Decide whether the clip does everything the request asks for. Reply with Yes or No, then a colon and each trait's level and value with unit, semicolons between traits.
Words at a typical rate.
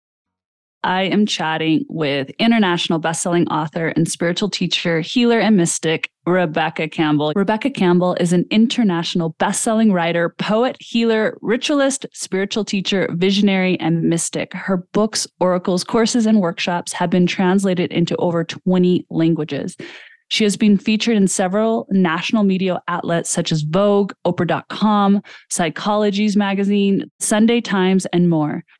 No: slow, 130 wpm